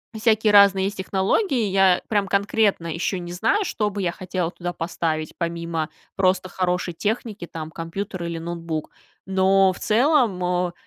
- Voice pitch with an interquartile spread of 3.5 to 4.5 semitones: No, average, 3.1 semitones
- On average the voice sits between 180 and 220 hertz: Yes, medium, 185 Hz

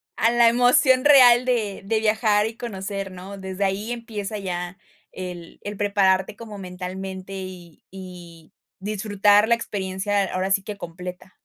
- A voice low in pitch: No, high, 195 Hz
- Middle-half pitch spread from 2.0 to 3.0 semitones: Yes, narrow, 2.6 semitones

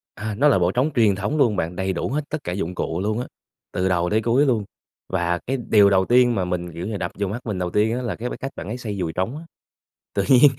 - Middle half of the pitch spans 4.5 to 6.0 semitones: Yes, average, 5.0 semitones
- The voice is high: No, low, 105 Hz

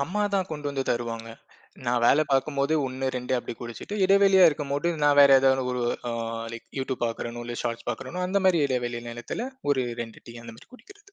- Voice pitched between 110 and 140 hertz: Yes, low, 135 Hz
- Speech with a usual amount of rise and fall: No, wide, 6.3 semitones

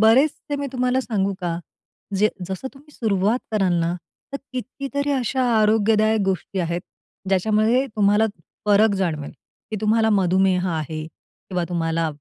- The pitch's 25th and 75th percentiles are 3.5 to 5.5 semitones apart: Yes, average, 4.6 semitones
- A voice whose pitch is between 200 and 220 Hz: Yes, high, 210 Hz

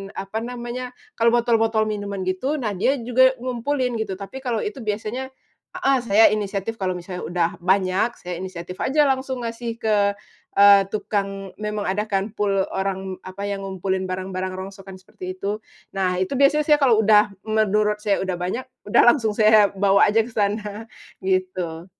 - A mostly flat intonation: No, average, 3.4 semitones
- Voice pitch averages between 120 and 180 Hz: No, high, 205 Hz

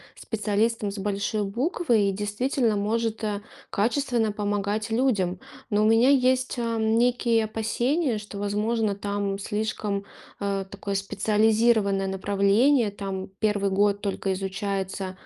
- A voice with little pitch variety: Yes, narrow, 2.3 semitones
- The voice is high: Yes, high, 210 Hz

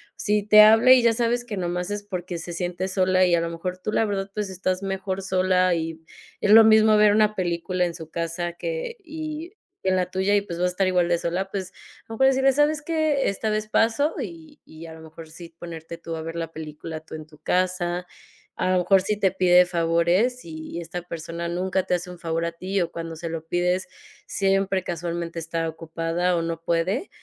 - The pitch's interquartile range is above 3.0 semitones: Yes, average, 3.5 semitones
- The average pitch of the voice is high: No, medium, 180 Hz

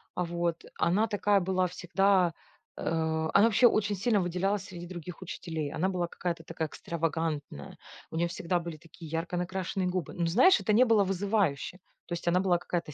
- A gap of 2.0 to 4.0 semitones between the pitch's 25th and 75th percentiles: Yes, average, 2.7 semitones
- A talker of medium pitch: Yes, medium, 175 Hz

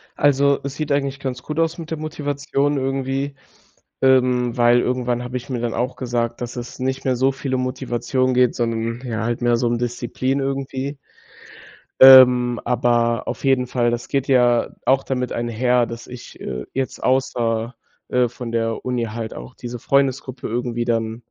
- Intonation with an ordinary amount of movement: No, narrow, 2.0 semitones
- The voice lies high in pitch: No, low, 125 Hz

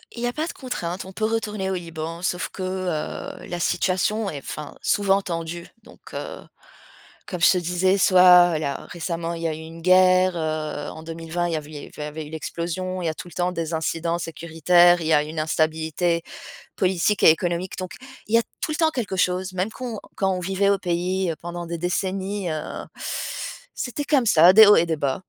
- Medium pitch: Yes, medium, 175 Hz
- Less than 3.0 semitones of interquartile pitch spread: Yes, narrow, 2.5 semitones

